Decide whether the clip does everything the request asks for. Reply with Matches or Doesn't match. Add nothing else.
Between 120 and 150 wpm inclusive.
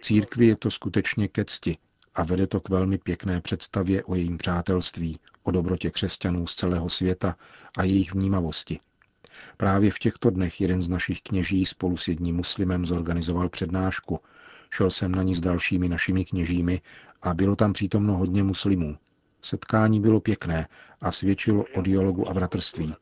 Doesn't match